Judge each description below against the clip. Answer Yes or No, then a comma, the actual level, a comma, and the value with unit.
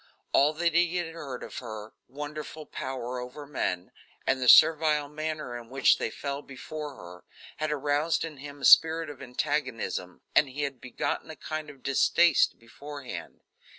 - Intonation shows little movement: No, average, 3.3 semitones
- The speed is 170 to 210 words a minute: No, average, 160 wpm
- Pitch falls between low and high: Yes, medium, 145 Hz